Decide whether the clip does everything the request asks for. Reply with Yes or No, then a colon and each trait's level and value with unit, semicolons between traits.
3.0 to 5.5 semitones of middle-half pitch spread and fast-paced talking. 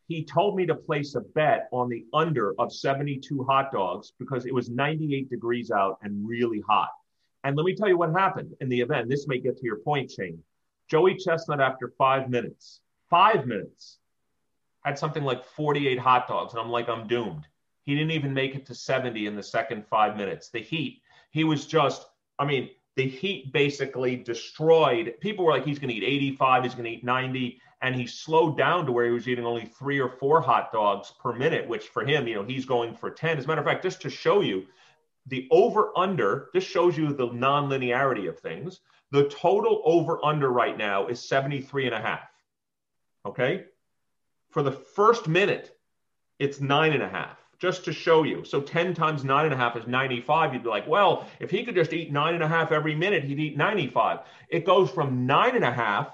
Yes: average, 4.2 semitones; fast, 210 wpm